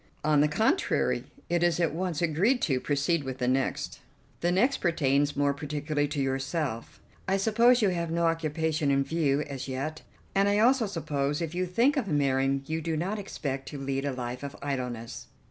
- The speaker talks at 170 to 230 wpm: Yes, average, 190 wpm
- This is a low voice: No, medium, 150 Hz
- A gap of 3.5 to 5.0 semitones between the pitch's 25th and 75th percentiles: Yes, average, 4.1 semitones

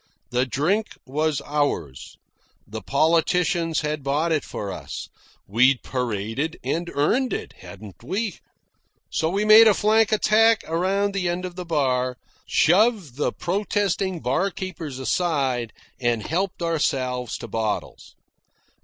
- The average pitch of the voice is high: No, medium, 160 Hz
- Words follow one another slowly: Yes, slow, 125 wpm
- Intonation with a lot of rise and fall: Yes, wide, 6.7 semitones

